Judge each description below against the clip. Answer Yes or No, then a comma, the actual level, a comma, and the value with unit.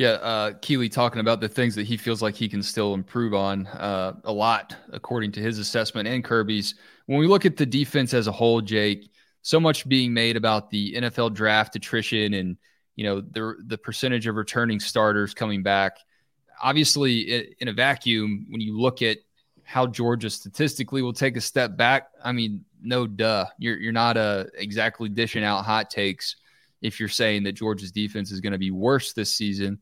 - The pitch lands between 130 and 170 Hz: No, low, 110 Hz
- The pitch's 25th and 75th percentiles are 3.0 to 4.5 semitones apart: No, narrow, 2.6 semitones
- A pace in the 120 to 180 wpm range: No, average, 195 wpm